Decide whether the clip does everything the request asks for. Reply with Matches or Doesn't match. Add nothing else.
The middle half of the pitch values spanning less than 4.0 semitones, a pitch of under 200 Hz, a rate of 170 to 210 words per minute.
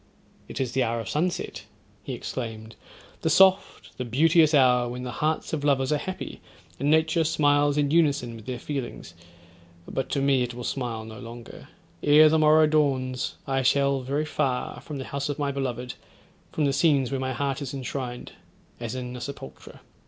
Matches